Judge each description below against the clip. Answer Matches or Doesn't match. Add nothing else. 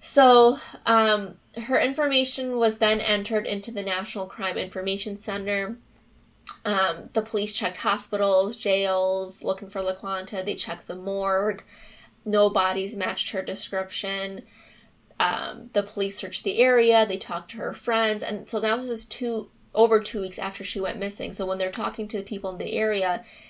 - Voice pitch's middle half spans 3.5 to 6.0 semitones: Doesn't match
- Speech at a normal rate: Matches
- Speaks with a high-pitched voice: Matches